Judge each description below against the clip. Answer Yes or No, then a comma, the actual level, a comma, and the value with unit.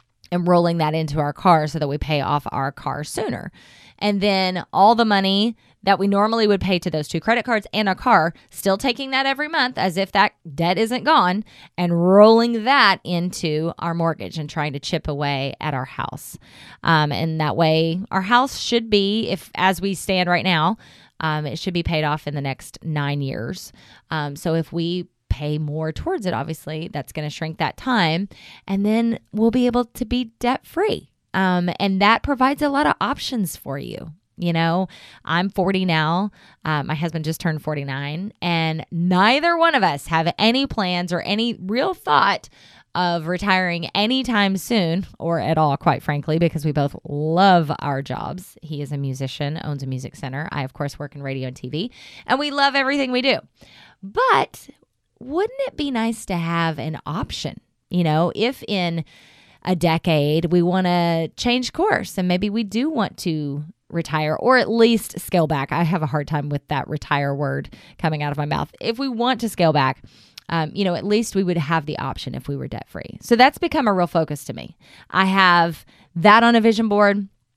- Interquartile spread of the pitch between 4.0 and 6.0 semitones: Yes, wide, 5.4 semitones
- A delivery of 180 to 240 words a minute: Yes, average, 200 wpm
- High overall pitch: No, medium, 175 Hz